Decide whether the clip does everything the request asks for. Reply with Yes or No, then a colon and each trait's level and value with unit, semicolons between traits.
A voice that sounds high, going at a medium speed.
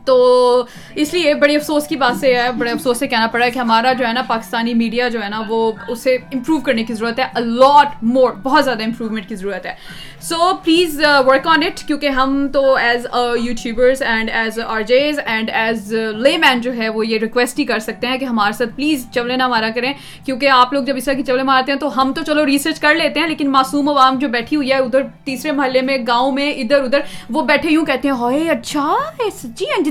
No: very high, 260 Hz; fast, 235 wpm